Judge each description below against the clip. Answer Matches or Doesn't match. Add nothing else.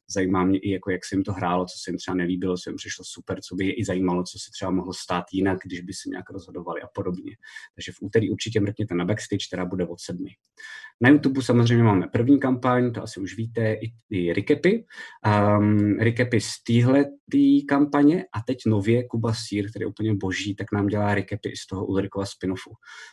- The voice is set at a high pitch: Doesn't match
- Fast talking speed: Matches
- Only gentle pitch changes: Doesn't match